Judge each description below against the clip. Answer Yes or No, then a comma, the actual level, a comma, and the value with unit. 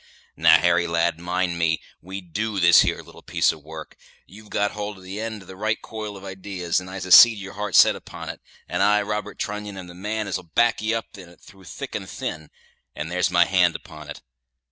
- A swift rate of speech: Yes, fast, 235 wpm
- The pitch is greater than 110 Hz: No, very low, 95 Hz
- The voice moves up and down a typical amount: Yes, average, 3.0 semitones